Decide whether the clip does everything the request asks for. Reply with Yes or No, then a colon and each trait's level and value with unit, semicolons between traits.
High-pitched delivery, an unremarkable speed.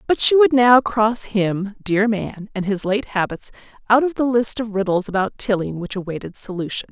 Yes: high, 210 Hz; average, 180 wpm